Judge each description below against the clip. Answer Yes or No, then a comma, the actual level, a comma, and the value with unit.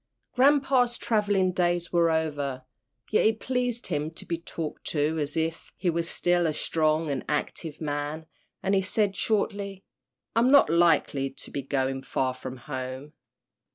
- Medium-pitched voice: Yes, medium, 165 Hz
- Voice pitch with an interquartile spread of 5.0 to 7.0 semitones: Yes, average, 5.3 semitones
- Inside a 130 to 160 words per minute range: Yes, average, 155 wpm